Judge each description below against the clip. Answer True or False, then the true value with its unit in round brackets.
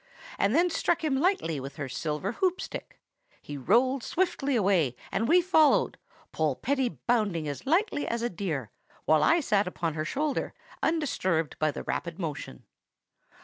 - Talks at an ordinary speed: True (155 wpm)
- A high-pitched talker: True (210 Hz)